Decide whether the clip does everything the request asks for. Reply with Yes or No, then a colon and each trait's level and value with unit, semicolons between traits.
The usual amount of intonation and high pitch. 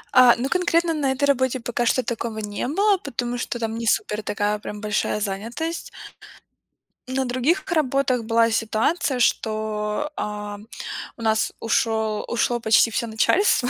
Yes: average, 3.5 semitones; high, 235 Hz